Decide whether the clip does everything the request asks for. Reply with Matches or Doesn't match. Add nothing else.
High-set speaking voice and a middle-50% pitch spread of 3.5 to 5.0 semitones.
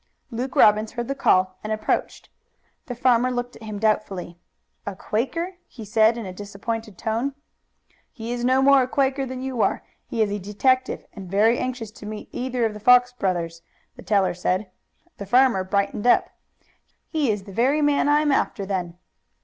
Matches